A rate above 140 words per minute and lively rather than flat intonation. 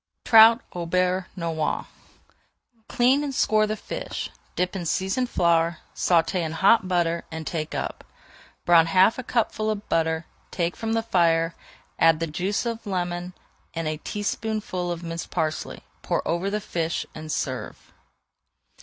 No: average, 155 wpm; average, 4.3 semitones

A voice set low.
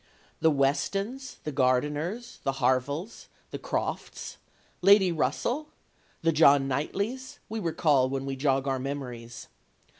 No: medium, 145 Hz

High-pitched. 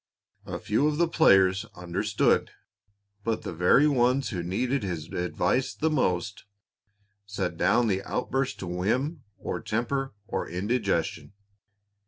No: low, 105 Hz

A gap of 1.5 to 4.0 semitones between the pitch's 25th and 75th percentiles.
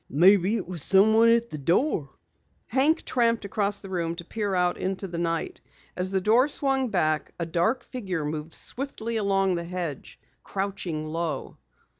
No: average, 5.0 semitones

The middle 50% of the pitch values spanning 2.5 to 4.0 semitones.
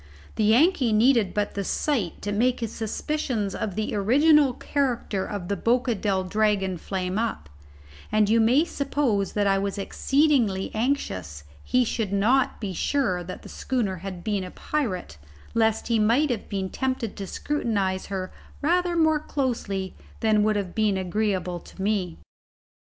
No: average, 4.6 semitones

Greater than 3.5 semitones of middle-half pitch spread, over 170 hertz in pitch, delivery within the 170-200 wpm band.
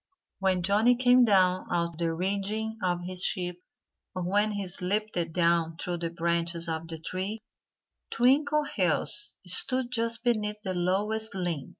No: average, 4.0 semitones; medium, 185 Hz; average, 150 wpm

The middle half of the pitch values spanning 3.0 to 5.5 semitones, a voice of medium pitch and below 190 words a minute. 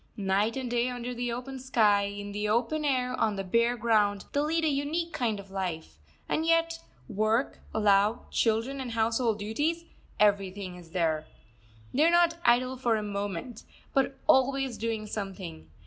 No: average, 4.5 semitones; high, 230 Hz; average, 165 wpm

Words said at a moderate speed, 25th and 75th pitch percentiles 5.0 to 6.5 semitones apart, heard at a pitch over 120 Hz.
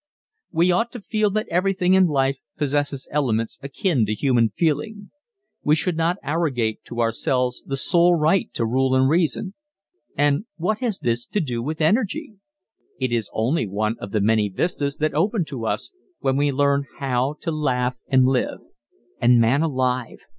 Yes: average, 170 wpm; wide, 5.6 semitones; medium, 140 Hz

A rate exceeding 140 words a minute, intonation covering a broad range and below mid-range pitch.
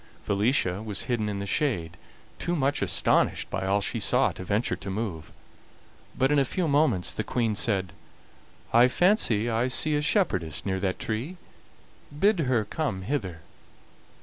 Yes: average, 160 wpm; wide, 6.5 semitones; low, 110 Hz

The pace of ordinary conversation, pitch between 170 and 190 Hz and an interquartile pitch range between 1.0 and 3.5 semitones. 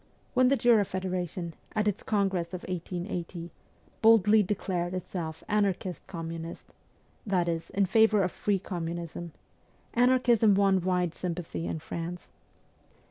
No: slow, 125 wpm; medium, 185 Hz; average, 3.2 semitones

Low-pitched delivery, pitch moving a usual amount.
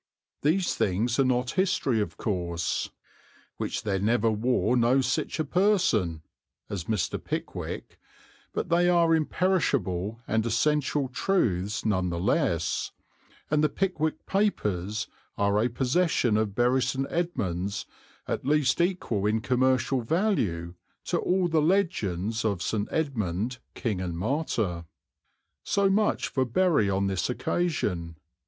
No: low, 120 Hz; wide, 7.9 semitones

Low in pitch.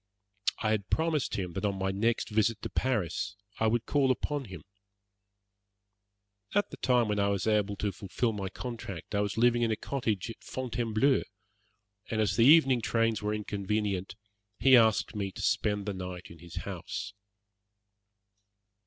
Yes: low, 110 Hz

